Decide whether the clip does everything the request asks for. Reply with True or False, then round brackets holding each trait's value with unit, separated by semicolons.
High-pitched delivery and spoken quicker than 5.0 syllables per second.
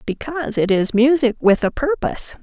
True (250 Hz; 5.4 syllables/s)